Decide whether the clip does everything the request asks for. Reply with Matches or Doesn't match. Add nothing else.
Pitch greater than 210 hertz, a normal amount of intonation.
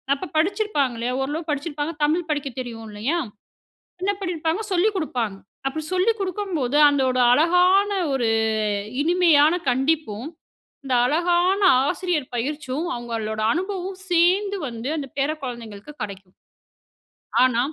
Doesn't match